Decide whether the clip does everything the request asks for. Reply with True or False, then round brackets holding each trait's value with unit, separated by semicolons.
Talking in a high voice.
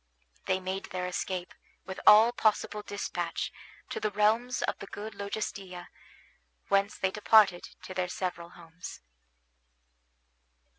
True (195 Hz)